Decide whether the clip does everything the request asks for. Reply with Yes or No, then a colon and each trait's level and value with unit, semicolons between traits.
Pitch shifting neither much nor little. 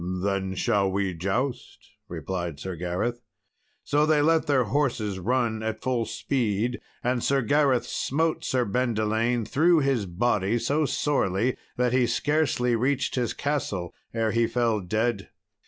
Yes: average, 4.9 semitones